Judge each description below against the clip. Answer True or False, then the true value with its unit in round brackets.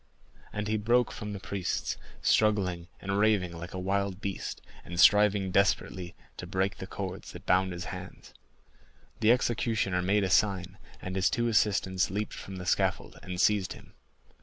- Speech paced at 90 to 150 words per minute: False (165 wpm)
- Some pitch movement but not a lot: False (2.2 semitones)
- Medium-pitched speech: False (95 Hz)